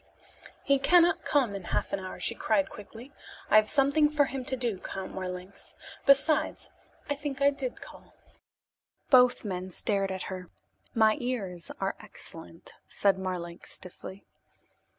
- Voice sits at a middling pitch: No, high, 220 Hz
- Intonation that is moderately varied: No, wide, 6.6 semitones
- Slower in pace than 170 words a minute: Yes, average, 150 wpm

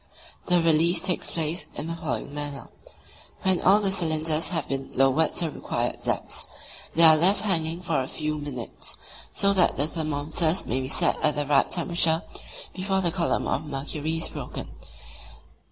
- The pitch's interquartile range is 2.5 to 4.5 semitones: Yes, average, 2.9 semitones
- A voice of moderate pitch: Yes, medium, 160 Hz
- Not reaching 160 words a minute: No, average, 170 wpm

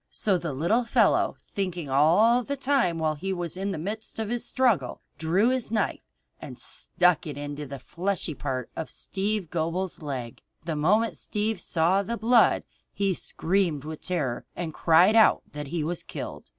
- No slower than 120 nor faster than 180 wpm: Yes, average, 175 wpm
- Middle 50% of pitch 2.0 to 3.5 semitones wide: No, wide, 5.4 semitones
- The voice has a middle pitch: Yes, medium, 180 Hz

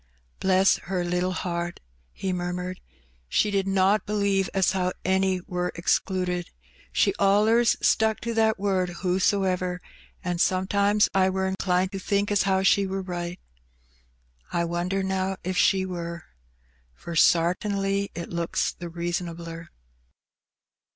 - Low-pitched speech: No, medium, 185 Hz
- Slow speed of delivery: Yes, slow, 130 wpm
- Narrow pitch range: Yes, narrow, 1.8 semitones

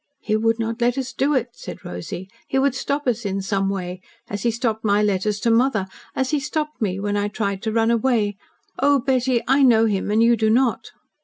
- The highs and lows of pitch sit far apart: No, average, 4.0 semitones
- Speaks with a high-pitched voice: Yes, high, 225 Hz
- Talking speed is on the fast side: Yes, fast, 225 wpm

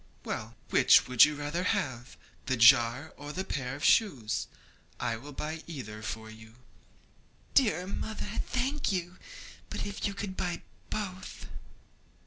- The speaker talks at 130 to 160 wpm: Yes, average, 140 wpm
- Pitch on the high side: No, medium, 150 Hz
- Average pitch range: No, wide, 7.8 semitones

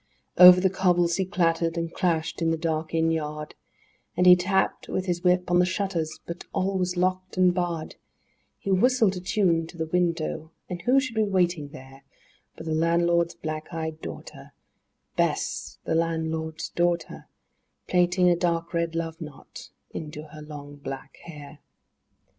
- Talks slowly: No, average, 165 wpm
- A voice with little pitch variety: Yes, narrow, 2.2 semitones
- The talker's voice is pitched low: No, medium, 170 Hz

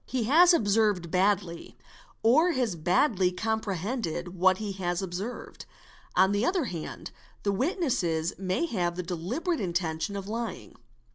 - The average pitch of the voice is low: No, high, 200 Hz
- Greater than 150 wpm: No, slow, 135 wpm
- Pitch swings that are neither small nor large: Yes, average, 5.0 semitones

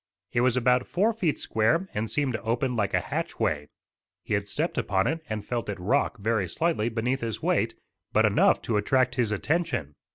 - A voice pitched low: Yes, low, 120 Hz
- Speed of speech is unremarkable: Yes, average, 195 wpm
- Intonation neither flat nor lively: Yes, average, 4.2 semitones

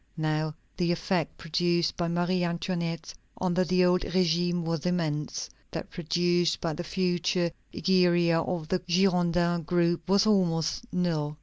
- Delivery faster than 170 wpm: No, slow, 135 wpm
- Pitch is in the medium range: Yes, medium, 175 Hz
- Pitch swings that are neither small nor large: No, narrow, 1.4 semitones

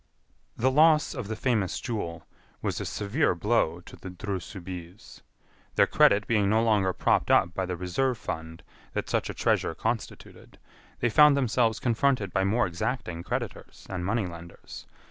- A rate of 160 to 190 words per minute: Yes, average, 165 wpm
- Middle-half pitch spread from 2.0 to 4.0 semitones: No, average, 4.9 semitones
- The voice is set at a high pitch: No, low, 105 Hz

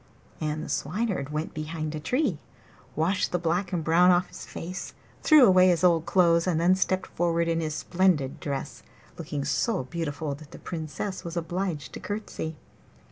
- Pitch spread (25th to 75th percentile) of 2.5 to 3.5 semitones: Yes, average, 3.0 semitones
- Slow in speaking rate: No, average, 175 wpm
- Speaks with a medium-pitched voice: Yes, medium, 170 Hz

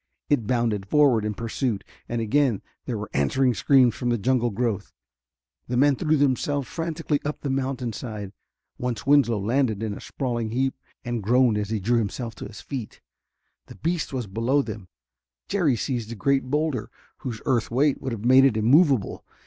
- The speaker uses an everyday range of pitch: Yes, average, 3.7 semitones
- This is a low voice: Yes, low, 125 Hz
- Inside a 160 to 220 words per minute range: Yes, average, 175 wpm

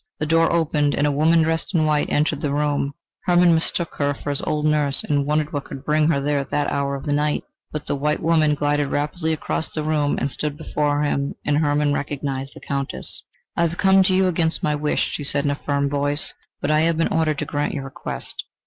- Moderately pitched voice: Yes, medium, 150 Hz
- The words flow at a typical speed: No, fast, 235 wpm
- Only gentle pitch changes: Yes, narrow, 1.6 semitones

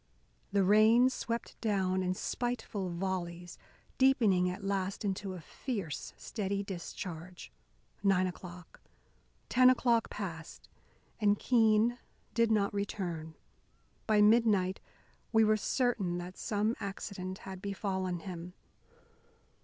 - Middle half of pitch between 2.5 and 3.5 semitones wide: Yes, average, 3.1 semitones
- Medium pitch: No, high, 195 Hz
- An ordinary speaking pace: No, slow, 110 wpm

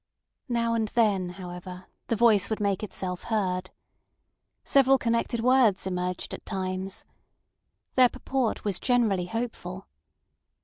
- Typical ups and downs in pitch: Yes, average, 4.1 semitones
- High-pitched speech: Yes, high, 210 Hz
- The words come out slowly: Yes, slow, 120 wpm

